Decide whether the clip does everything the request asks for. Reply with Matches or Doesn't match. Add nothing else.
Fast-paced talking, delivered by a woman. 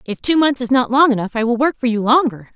Matches